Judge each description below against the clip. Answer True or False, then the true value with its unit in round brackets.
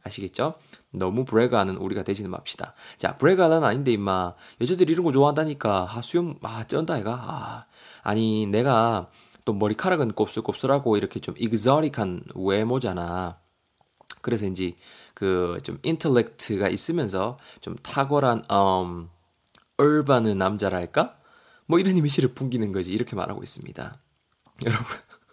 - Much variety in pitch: True (6.6 semitones)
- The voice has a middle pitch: False (110 Hz)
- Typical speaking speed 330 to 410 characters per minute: False (315 characters per minute)